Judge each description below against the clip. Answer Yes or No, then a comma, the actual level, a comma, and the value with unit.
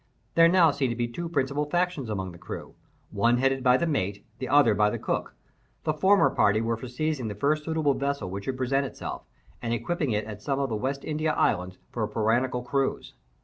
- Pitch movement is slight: No, average, 5.1 semitones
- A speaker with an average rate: No, fast, 215 wpm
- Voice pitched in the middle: No, low, 130 Hz